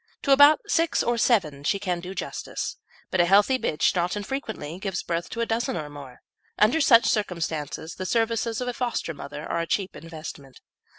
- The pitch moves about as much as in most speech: No, wide, 6.2 semitones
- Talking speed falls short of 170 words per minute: No, average, 190 wpm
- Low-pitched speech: No, high, 190 Hz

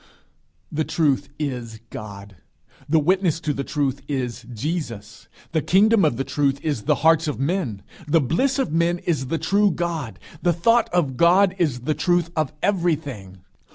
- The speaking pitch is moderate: Yes, medium, 155 Hz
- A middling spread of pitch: Yes, average, 4.9 semitones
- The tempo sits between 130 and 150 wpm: No, average, 165 wpm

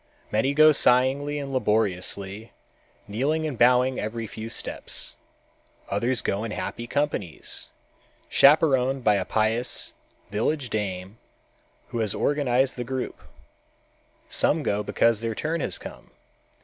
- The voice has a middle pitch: No, low, 120 Hz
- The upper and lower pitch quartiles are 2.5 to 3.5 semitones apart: No, average, 4.3 semitones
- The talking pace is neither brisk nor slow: No, slow, 125 wpm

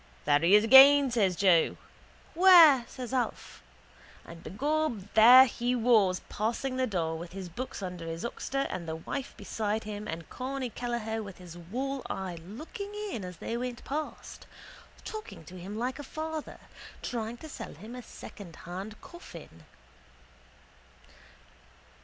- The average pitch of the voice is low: No, high, 225 Hz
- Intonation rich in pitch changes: Yes, wide, 6.2 semitones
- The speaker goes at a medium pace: Yes, average, 150 wpm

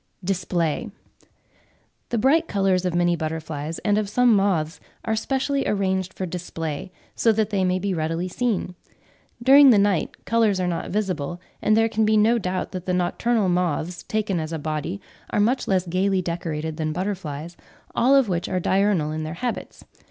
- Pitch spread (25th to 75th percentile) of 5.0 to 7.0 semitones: No, average, 4.0 semitones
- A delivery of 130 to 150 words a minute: No, average, 175 wpm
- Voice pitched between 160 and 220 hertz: Yes, medium, 185 Hz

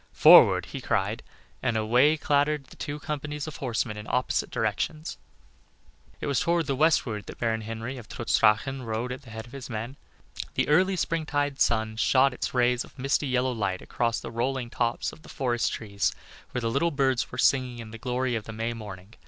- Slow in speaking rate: No, average, 200 wpm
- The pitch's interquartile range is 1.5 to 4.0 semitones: Yes, average, 3.7 semitones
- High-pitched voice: No, low, 125 Hz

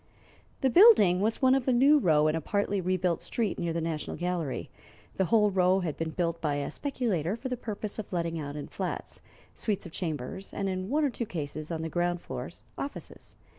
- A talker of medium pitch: Yes, medium, 180 Hz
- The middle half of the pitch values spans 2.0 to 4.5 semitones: No, average, 5.2 semitones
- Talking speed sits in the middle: No, fast, 210 wpm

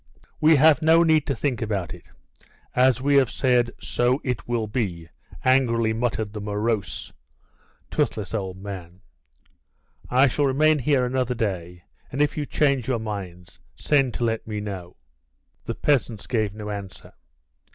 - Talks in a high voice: No, low, 115 Hz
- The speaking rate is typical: Yes, average, 150 wpm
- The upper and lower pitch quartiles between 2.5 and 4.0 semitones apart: No, average, 4.6 semitones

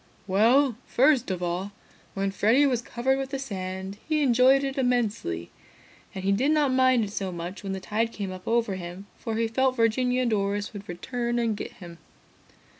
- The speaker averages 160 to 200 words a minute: Yes, average, 190 wpm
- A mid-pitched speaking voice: No, high, 225 Hz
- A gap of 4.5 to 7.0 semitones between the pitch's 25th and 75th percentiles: Yes, average, 4.8 semitones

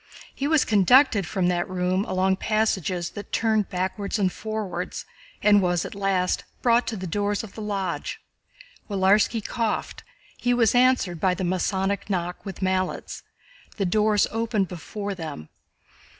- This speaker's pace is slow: No, average, 150 wpm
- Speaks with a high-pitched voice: Yes, high, 195 Hz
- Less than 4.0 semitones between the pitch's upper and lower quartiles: Yes, average, 2.9 semitones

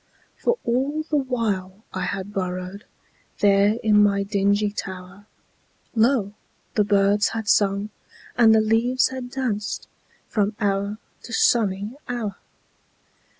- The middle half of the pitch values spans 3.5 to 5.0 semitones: No, narrow, 2.6 semitones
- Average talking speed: No, slow, 110 wpm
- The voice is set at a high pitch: Yes, high, 205 Hz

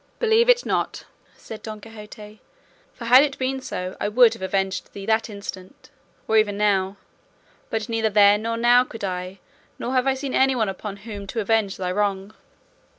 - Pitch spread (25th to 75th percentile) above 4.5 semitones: No, average, 3.3 semitones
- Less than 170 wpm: No, average, 180 wpm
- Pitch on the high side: Yes, high, 215 Hz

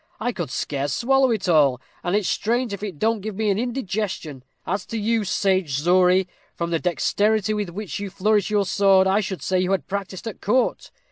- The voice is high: Yes, high, 195 Hz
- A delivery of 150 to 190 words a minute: No, fast, 205 wpm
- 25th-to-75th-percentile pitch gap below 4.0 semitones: Yes, average, 3.1 semitones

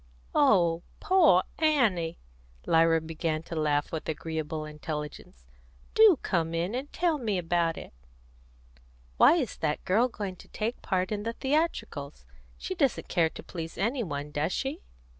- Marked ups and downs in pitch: Yes, wide, 7.5 semitones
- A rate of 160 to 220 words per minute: No, average, 150 wpm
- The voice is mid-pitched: Yes, medium, 175 Hz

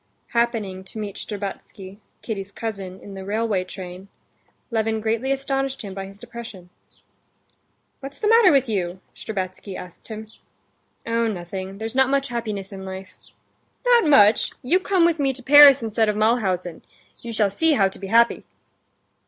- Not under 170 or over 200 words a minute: No, average, 160 wpm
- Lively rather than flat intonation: No, average, 4.7 semitones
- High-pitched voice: Yes, high, 220 Hz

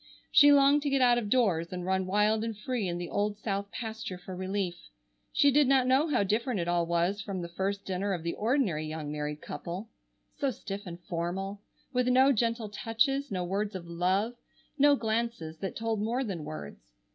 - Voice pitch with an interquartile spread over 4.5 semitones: Yes, average, 5.2 semitones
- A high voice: Yes, high, 205 Hz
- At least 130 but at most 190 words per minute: No, average, 200 wpm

